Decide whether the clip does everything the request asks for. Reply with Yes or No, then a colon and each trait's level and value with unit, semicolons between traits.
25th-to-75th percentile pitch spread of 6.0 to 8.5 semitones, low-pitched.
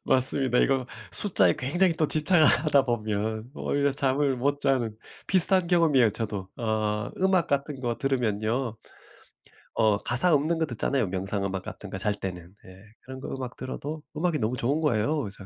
No: average, 5.3 semitones; low, 130 Hz